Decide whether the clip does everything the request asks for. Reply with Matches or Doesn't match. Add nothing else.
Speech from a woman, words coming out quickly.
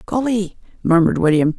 Doesn't match